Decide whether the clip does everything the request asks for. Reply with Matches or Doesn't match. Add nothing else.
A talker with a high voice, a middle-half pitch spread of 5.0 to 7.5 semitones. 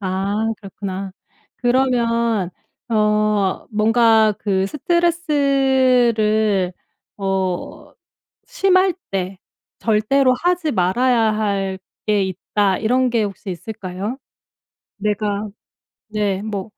Doesn't match